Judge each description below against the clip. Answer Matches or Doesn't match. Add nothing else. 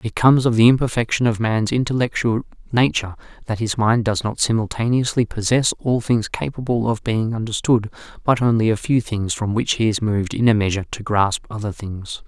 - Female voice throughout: Doesn't match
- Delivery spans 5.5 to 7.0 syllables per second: Matches